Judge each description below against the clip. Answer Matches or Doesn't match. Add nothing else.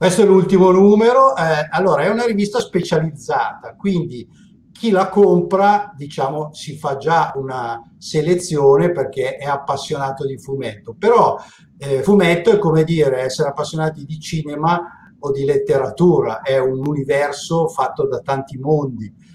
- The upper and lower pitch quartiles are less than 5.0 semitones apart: Doesn't match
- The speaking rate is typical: Matches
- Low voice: Doesn't match